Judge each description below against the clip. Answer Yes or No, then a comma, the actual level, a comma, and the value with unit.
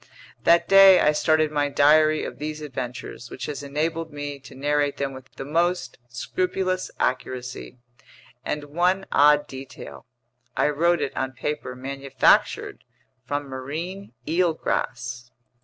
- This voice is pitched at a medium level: Yes, medium, 145 Hz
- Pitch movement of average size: Yes, average, 3.6 semitones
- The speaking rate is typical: No, slow, 130 wpm